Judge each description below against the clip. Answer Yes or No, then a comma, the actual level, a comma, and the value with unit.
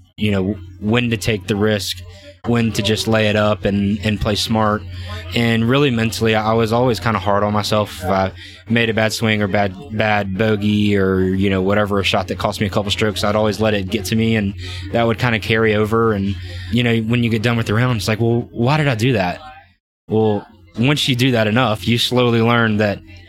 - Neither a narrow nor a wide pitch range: No, narrow, 2.2 semitones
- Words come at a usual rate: No, fast, 235 wpm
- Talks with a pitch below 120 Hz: Yes, low, 110 Hz